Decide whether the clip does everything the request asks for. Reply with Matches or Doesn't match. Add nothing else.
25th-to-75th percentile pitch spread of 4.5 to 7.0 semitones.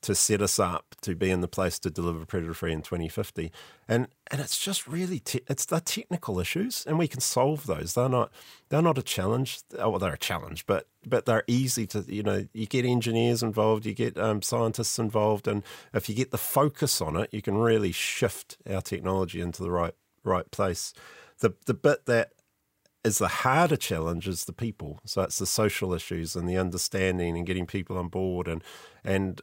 Matches